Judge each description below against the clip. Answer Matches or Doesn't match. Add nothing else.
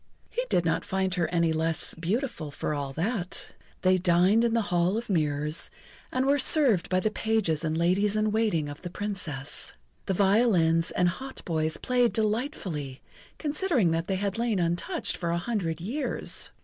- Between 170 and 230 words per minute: Matches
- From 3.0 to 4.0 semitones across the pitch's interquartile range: Doesn't match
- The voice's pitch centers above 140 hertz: Matches